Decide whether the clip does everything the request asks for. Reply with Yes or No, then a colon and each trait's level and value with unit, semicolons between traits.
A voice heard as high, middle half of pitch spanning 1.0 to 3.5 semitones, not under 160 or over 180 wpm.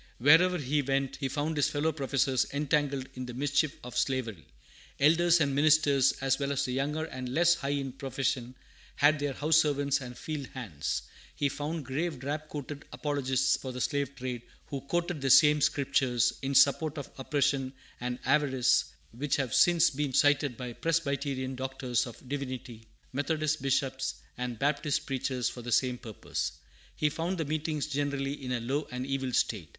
No: medium, 140 Hz; narrow, 2.4 semitones; average, 170 wpm